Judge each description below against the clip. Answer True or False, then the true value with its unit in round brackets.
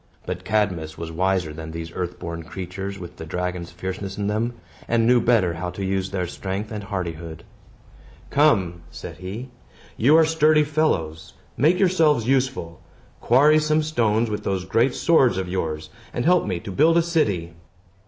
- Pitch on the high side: False (100 Hz)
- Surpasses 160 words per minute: True (170 wpm)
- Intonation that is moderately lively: False (6.8 semitones)